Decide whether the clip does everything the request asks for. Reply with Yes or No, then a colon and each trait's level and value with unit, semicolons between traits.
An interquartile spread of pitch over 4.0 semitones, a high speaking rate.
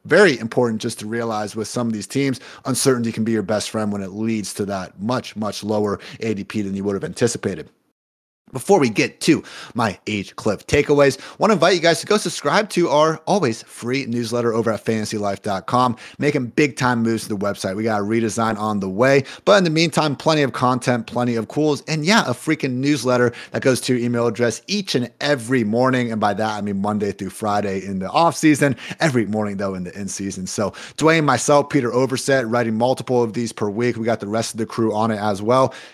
Yes: average, 4.5 semitones; fast, 225 wpm